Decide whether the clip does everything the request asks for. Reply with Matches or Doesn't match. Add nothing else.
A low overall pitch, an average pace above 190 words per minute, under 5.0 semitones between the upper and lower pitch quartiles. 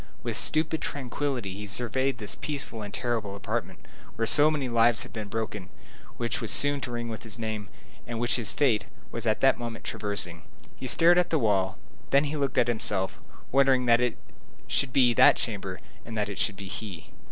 Matches